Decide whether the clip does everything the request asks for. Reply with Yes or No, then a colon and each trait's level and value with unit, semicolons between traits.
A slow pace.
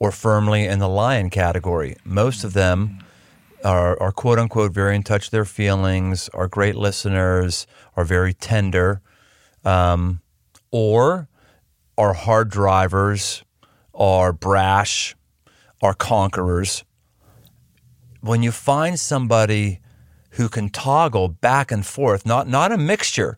Yes: slow, 125 wpm